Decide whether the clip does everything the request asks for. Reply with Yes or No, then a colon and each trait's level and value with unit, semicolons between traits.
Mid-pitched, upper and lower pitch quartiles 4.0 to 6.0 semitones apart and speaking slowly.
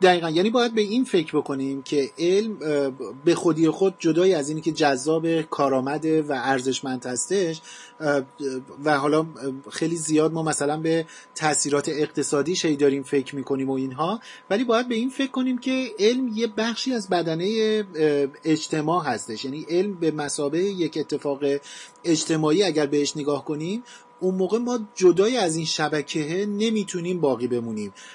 No: medium, 160 Hz; average, 5.1 semitones; average, 150 wpm